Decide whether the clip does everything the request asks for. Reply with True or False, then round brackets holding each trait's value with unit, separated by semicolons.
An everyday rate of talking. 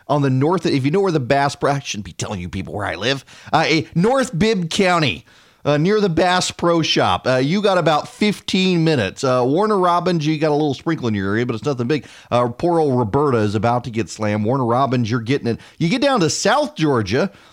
False (245 wpm)